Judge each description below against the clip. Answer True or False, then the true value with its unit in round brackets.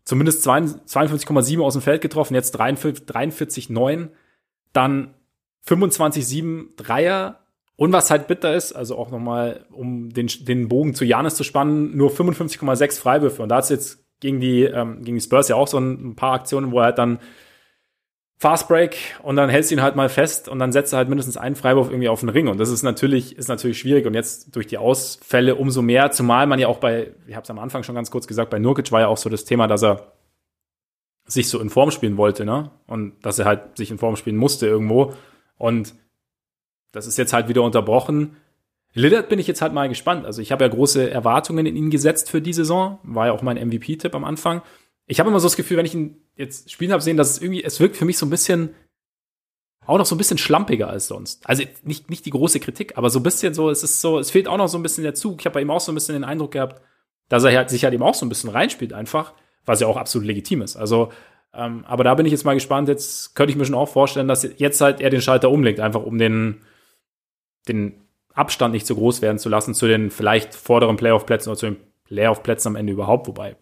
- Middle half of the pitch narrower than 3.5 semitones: False (4.4 semitones)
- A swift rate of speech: True (235 wpm)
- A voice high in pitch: False (130 Hz)